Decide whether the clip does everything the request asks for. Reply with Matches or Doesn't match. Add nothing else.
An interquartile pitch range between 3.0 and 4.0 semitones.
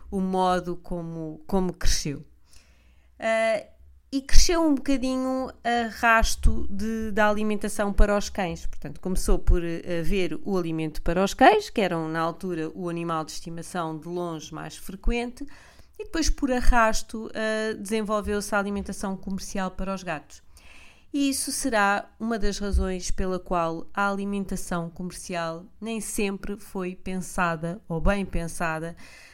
Doesn't match